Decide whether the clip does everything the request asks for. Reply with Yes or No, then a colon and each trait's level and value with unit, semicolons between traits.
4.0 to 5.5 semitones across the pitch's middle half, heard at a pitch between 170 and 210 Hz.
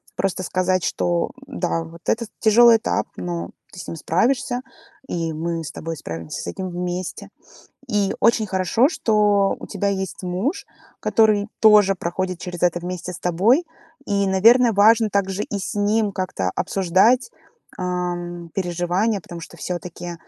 No: average, 3.3 semitones; high, 190 Hz